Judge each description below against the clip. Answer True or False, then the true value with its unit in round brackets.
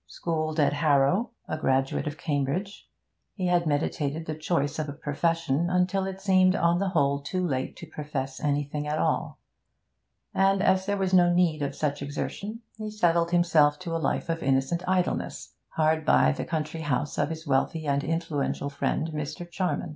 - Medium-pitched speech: True (160 Hz)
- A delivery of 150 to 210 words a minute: True (175 wpm)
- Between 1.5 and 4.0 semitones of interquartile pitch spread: True (3.6 semitones)